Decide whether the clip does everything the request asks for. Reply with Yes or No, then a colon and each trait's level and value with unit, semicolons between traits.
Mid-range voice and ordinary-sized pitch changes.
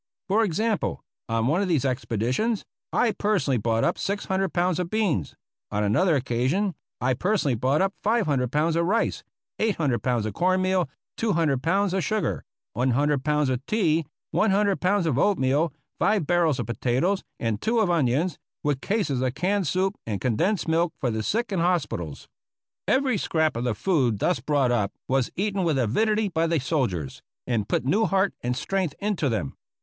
No: medium, 160 Hz; wide, 7.3 semitones